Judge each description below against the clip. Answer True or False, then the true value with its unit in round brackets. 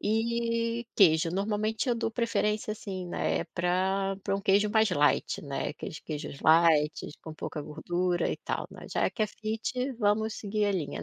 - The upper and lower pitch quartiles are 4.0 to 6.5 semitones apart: True (4.7 semitones)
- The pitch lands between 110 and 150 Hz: False (200 Hz)